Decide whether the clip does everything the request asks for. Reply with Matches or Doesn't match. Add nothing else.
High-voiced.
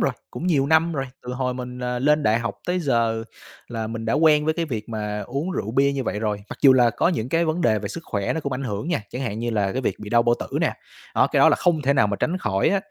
Doesn't match